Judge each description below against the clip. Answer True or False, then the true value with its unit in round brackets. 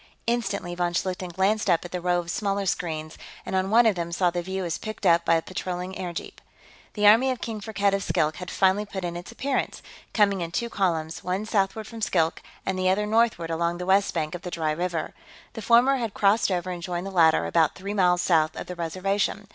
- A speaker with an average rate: False (230 wpm)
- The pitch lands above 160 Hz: True (185 Hz)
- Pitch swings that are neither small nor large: True (3.1 semitones)